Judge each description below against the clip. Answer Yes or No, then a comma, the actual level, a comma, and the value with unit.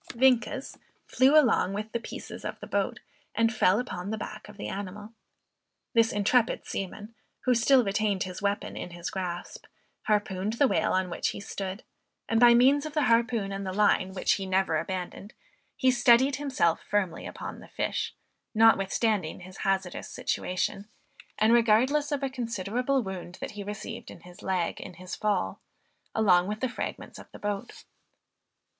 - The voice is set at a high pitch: Yes, high, 210 Hz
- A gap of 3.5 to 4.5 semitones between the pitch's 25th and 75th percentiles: Yes, average, 4.0 semitones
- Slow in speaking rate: No, average, 170 wpm